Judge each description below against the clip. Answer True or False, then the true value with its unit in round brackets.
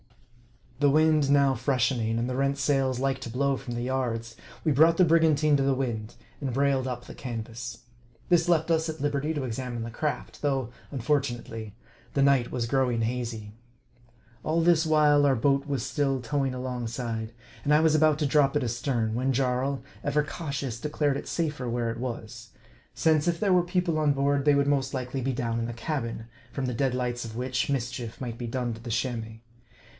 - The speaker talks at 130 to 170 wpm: False (200 wpm)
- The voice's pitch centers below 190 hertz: True (135 Hz)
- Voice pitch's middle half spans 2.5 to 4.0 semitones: True (3.4 semitones)